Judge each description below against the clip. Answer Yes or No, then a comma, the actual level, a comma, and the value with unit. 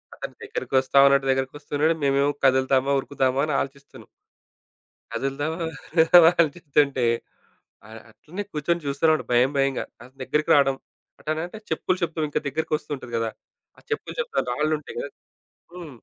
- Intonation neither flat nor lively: Yes, average, 3.0 semitones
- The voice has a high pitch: No, medium, 145 Hz